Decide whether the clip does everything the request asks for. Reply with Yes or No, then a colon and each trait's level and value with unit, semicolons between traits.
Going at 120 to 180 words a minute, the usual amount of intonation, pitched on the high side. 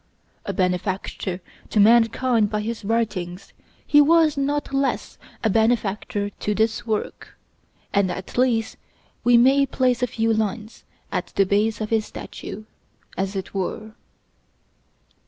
Yes: slow, 135 wpm; average, 3.3 semitones; high, 220 Hz